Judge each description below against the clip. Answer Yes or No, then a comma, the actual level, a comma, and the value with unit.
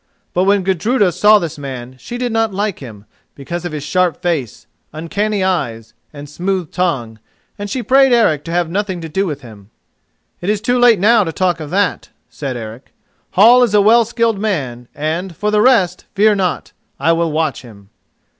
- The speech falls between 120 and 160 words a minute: No, average, 190 wpm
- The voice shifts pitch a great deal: Yes, wide, 6.0 semitones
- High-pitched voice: No, medium, 180 Hz